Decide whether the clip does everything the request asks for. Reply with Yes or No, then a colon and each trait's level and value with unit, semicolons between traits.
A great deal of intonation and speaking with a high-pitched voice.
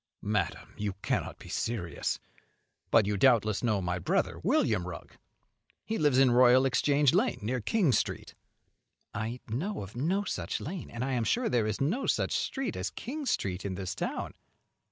No: wide, 6.6 semitones; low, 125 Hz